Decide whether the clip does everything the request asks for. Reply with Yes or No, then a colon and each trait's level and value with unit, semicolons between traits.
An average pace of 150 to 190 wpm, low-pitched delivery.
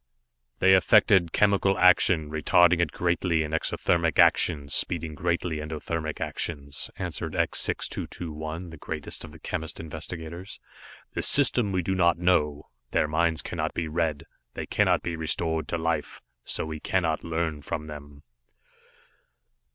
No: average, 140 wpm; very low, 80 Hz